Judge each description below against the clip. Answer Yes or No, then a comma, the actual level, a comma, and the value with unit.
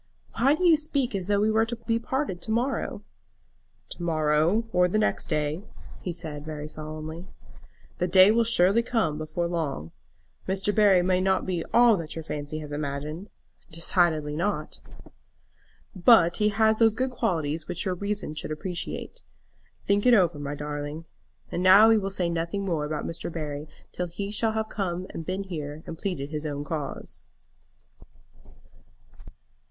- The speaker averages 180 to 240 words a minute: No, average, 160 wpm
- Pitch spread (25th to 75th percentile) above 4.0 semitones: Yes, average, 5.2 semitones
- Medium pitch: Yes, medium, 175 Hz